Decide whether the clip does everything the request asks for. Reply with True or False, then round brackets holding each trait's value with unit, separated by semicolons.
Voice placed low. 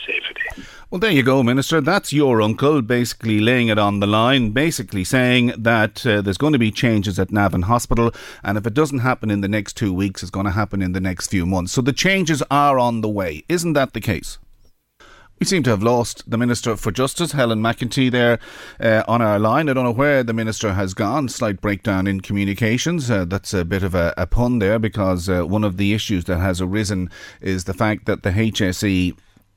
True (110 Hz)